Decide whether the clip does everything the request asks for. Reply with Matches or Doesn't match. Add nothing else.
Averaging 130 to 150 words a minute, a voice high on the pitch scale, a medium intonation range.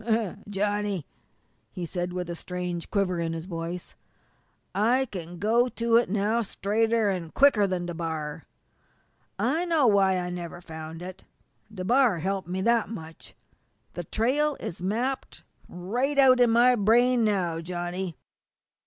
Matches